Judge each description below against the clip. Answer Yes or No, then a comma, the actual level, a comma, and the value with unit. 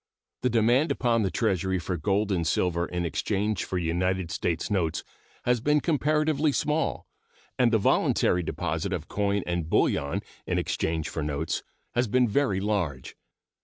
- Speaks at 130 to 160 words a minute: Yes, average, 155 wpm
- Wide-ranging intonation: Yes, wide, 5.8 semitones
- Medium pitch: No, very low, 95 Hz